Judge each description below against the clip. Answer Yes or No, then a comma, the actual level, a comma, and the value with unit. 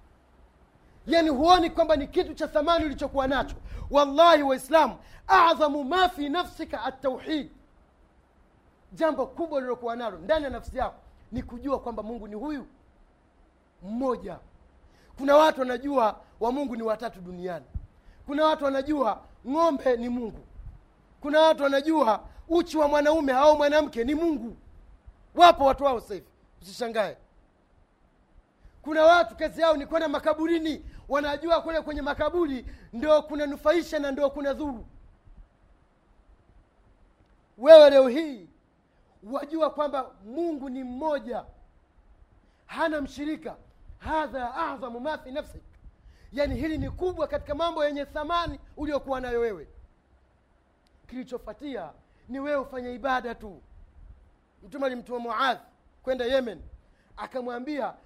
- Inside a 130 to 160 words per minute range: No, average, 120 wpm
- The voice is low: No, very high, 275 Hz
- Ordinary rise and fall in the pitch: Yes, average, 4.9 semitones